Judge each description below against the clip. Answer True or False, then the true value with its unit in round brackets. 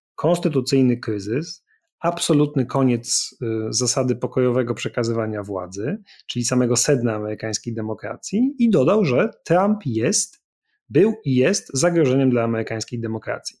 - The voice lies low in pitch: True (130 Hz)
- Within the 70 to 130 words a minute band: True (115 wpm)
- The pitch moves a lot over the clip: True (6.5 semitones)